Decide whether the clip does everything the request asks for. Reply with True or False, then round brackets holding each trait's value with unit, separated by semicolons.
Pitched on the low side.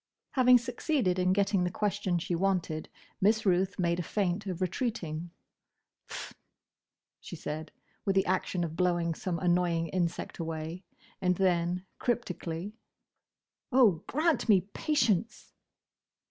False (185 Hz)